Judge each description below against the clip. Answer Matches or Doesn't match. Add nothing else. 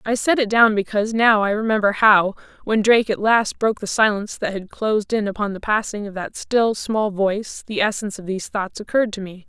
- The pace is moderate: Doesn't match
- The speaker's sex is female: Matches